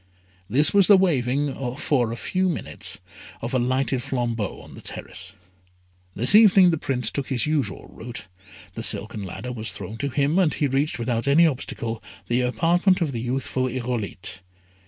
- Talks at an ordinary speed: Yes, average, 170 wpm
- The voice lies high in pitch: No, low, 130 Hz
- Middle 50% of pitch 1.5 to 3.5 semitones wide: No, average, 4.2 semitones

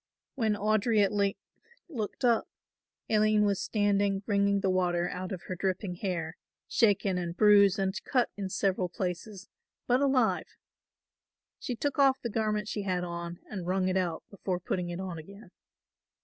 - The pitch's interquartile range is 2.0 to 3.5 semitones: Yes, average, 2.8 semitones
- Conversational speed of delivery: Yes, average, 165 wpm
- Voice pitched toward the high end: Yes, high, 200 Hz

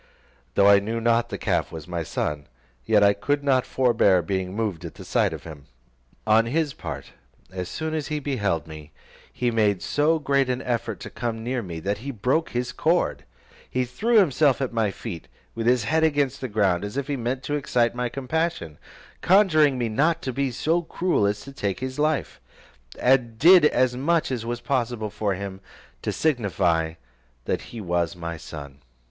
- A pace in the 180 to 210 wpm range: Yes, average, 190 wpm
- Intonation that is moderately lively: No, wide, 5.7 semitones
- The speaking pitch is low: Yes, low, 120 Hz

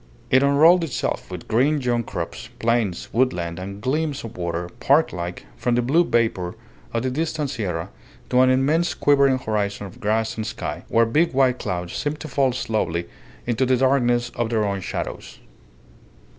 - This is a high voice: No, low, 120 Hz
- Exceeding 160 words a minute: Yes, average, 170 wpm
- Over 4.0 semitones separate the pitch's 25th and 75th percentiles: Yes, average, 4.8 semitones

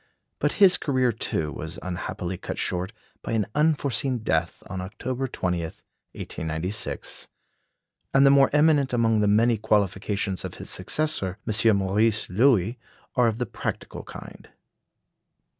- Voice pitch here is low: Yes, low, 110 Hz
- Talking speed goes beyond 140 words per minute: No, slow, 135 wpm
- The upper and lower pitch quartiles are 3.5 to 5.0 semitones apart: No, wide, 5.6 semitones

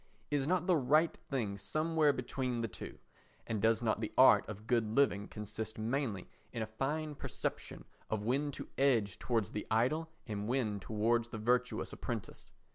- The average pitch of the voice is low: Yes, low, 115 Hz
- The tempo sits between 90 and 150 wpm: No, average, 170 wpm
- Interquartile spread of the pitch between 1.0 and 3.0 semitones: No, average, 4.2 semitones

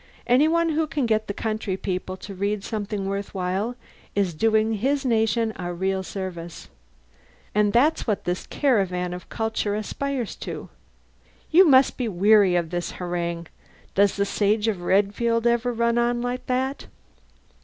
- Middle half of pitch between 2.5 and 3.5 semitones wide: No, average, 4.0 semitones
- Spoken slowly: No, average, 155 wpm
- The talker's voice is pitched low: No, high, 210 Hz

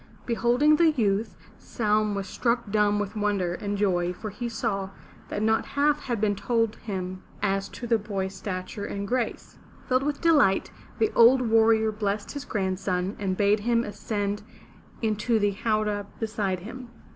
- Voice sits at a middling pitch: No, high, 210 Hz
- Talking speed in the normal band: Yes, average, 160 wpm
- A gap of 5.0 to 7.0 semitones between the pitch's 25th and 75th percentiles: No, average, 2.8 semitones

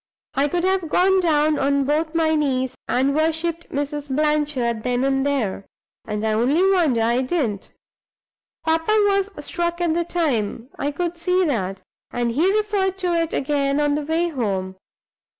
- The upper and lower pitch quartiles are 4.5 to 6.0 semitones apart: Yes, average, 4.9 semitones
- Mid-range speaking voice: No, very high, 295 Hz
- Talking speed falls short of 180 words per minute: Yes, average, 165 wpm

